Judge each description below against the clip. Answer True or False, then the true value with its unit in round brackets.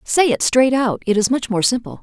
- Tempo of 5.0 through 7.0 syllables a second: True (5.3 syllables/s)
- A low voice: False (245 Hz)